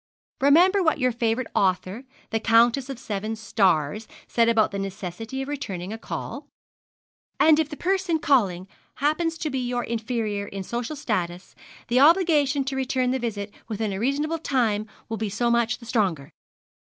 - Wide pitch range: No, average, 5.0 semitones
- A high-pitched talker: Yes, high, 235 Hz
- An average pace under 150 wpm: No, average, 165 wpm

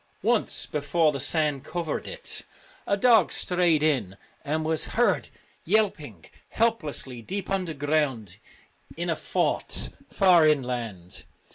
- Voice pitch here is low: No, medium, 155 Hz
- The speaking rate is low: Yes, slow, 115 wpm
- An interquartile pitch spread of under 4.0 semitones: No, average, 5.0 semitones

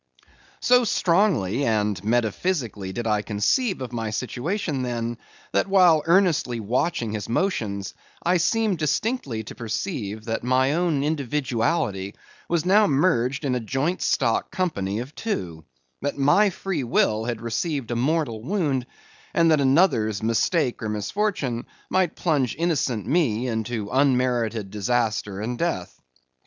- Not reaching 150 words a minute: Yes, slow, 135 wpm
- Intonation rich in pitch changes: Yes, wide, 7.0 semitones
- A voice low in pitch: Yes, low, 125 Hz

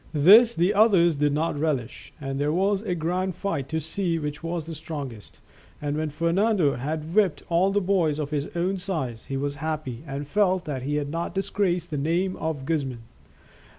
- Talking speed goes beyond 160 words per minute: Yes, average, 190 wpm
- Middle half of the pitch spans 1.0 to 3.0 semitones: No, average, 4.1 semitones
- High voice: No, medium, 160 Hz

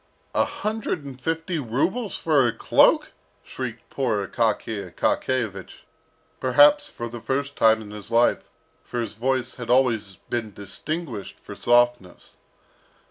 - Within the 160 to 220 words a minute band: No, slow, 135 wpm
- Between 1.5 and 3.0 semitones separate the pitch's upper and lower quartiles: No, average, 4.1 semitones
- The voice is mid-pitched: No, low, 120 Hz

